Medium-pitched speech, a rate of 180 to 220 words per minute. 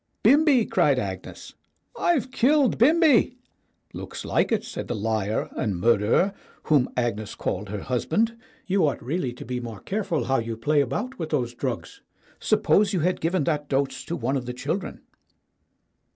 No: medium, 145 Hz; average, 165 wpm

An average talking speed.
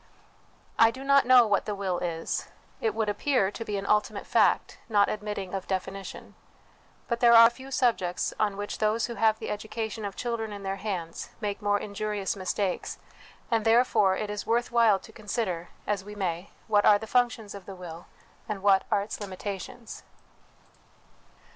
Yes: average, 180 wpm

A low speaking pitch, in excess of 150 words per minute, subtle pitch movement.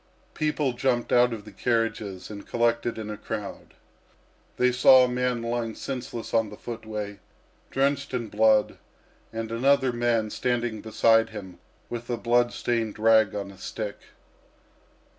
No: low, 115 Hz; average, 145 wpm; narrow, 2.1 semitones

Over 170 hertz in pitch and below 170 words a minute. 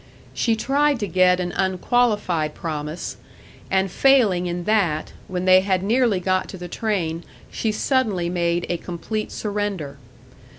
Yes: medium, 185 Hz; average, 140 wpm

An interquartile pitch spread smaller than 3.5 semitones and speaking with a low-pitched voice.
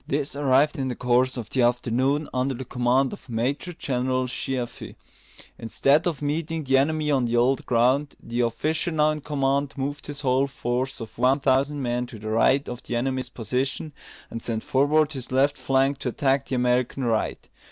Yes: narrow, 2.6 semitones; low, 130 Hz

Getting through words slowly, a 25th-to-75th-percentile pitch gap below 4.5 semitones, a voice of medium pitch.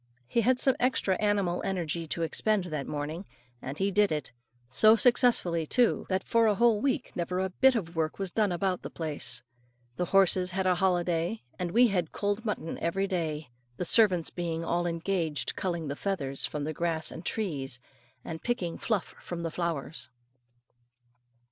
No: average, 180 wpm; average, 3.8 semitones; medium, 180 Hz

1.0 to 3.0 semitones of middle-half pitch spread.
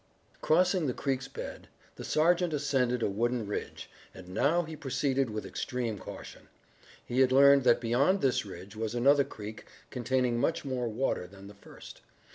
No: average, 3.9 semitones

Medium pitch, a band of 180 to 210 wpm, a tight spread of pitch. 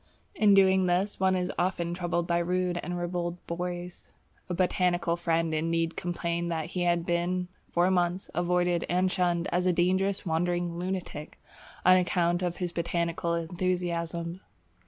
No: medium, 175 Hz; average, 150 wpm; narrow, 1.1 semitones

